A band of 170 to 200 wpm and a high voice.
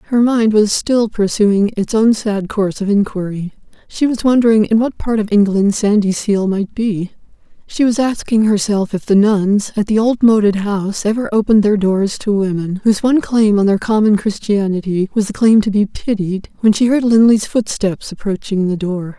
Yes: average, 190 wpm; high, 210 Hz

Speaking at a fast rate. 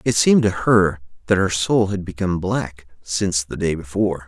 No: average, 195 wpm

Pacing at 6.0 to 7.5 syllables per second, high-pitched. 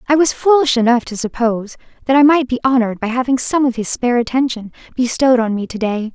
Yes: 6.5 syllables/s; high, 245 Hz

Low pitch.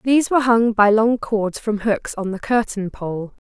No: high, 215 Hz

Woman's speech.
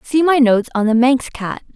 Yes: female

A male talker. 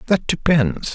Yes: male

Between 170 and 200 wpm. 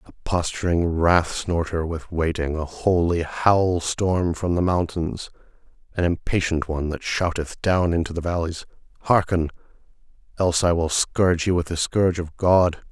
No: average, 155 wpm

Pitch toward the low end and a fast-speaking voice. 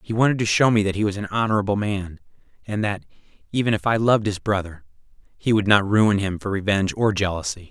Yes: low, 100 Hz; fast, 220 wpm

